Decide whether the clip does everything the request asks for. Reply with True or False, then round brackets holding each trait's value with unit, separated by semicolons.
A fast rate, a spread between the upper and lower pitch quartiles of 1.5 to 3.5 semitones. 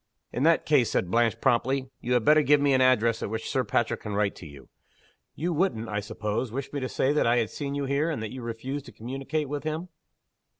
False (245 wpm; 4.2 semitones)